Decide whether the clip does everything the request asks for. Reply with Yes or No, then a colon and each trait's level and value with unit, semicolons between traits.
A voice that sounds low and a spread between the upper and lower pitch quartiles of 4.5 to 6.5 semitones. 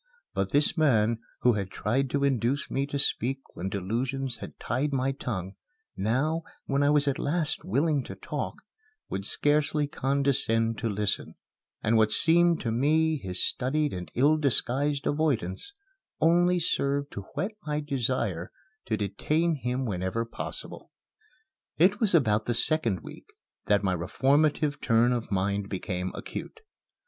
Yes: low, 130 Hz; wide, 5.4 semitones